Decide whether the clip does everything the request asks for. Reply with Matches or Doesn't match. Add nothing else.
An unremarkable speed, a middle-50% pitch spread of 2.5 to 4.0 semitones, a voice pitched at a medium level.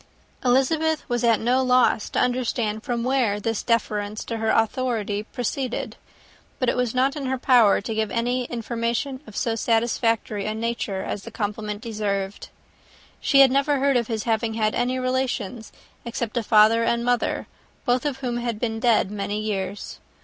Doesn't match